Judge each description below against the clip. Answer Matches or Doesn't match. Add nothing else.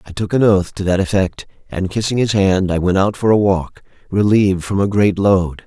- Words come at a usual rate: Doesn't match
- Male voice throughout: Matches